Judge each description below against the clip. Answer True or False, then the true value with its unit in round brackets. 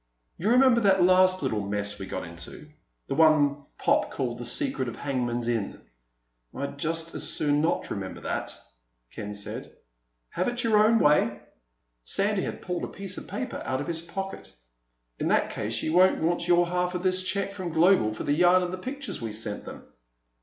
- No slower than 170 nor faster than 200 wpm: True (190 wpm)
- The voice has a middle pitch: True (165 Hz)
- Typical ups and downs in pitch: False (7.0 semitones)